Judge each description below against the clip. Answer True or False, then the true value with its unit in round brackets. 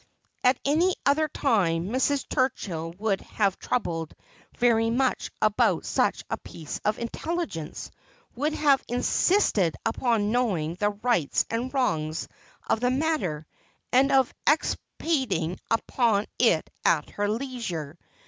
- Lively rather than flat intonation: True (6.6 semitones)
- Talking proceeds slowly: True (125 wpm)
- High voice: True (230 Hz)